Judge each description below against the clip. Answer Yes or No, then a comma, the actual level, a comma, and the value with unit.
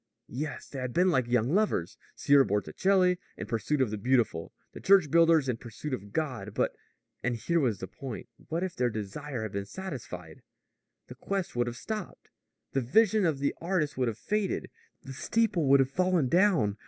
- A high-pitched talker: No, low, 135 Hz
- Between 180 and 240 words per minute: Yes, average, 190 wpm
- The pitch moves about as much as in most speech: No, wide, 7.0 semitones